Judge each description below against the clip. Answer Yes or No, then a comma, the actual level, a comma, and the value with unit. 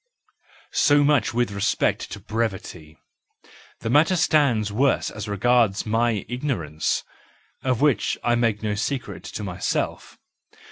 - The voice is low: Yes, low, 115 Hz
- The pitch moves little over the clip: No, average, 4.2 semitones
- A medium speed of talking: No, slow, 125 wpm